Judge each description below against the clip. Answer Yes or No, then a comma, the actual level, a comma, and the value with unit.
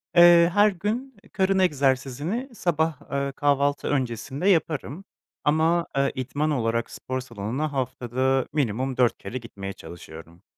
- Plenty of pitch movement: No, average, 5.0 semitones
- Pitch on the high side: No, medium, 140 Hz